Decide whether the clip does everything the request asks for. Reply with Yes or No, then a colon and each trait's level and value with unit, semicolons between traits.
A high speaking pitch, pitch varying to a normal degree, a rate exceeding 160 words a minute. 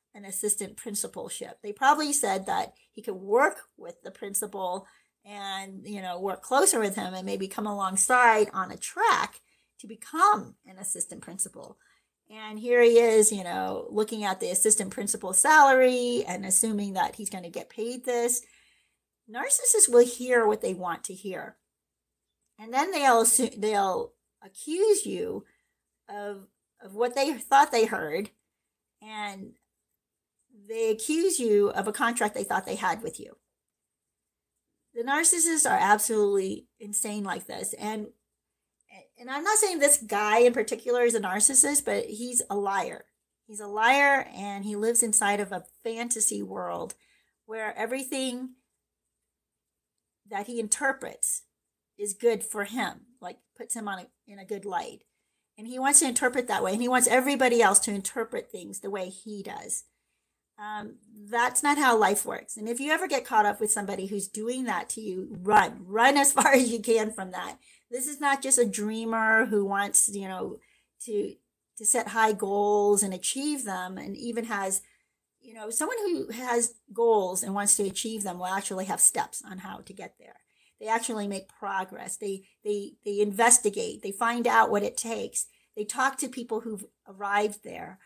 Yes: high, 220 Hz; average, 3.6 semitones; average, 170 wpm